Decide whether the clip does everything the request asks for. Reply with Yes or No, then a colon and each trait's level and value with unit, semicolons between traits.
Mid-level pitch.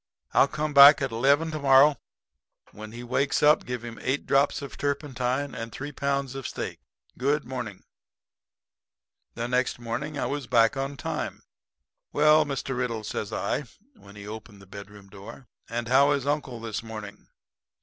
No: low, 130 Hz